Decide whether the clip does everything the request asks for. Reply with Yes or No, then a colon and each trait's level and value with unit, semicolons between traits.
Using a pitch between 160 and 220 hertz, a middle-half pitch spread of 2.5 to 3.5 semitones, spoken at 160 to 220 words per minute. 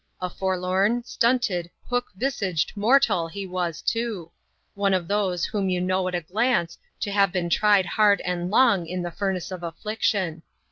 Yes: high, 190 Hz; average, 2.9 semitones; average, 170 wpm